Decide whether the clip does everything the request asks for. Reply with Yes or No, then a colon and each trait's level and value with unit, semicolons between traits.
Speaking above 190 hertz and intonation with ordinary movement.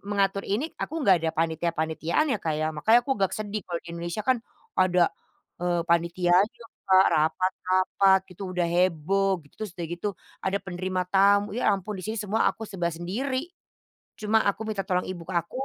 No: medium, 185 Hz; average, 3.0 semitones